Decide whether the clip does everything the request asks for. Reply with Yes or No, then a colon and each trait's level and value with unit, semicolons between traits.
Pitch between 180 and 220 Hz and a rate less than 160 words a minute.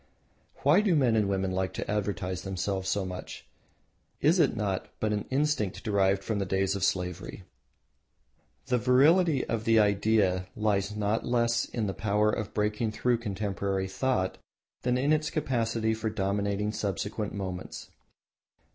No: low, 105 Hz; average, 150 wpm